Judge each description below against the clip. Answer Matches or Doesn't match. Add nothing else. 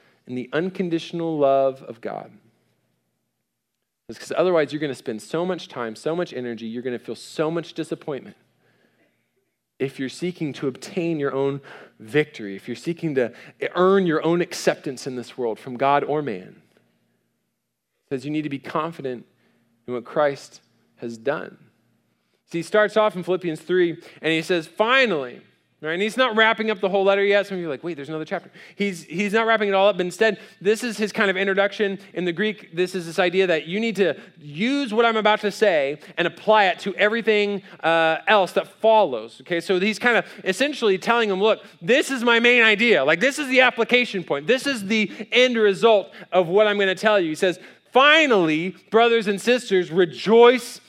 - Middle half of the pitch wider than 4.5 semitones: Matches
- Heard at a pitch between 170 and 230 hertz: Matches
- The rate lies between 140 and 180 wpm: Doesn't match